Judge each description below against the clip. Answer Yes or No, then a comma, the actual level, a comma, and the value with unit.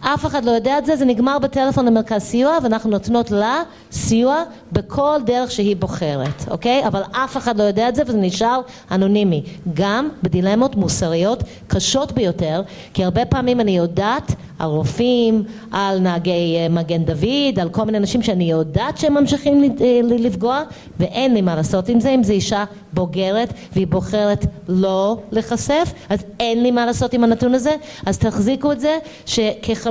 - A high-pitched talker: Yes, high, 220 Hz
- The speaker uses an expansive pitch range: No, average, 5.0 semitones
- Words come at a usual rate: No, fast, 165 wpm